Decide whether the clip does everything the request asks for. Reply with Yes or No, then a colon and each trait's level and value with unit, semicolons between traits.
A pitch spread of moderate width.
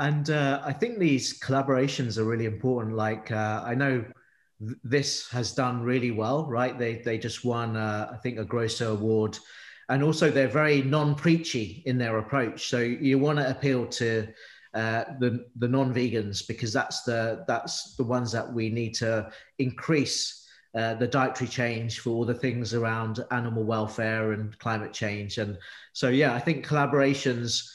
Yes: average, 3.1 semitones